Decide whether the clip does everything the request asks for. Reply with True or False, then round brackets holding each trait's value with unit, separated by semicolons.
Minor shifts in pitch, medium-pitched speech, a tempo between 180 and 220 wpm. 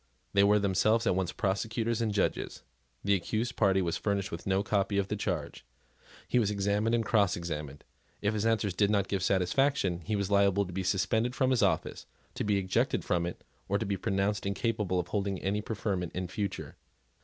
False (2.3 semitones; 100 Hz; 190 wpm)